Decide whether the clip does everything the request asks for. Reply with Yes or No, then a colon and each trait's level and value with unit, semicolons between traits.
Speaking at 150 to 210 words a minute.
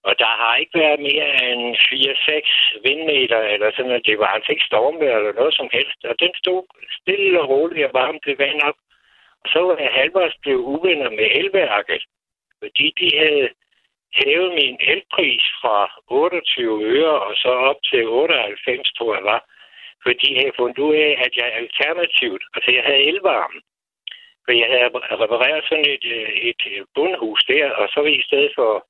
Yes: average, 180 wpm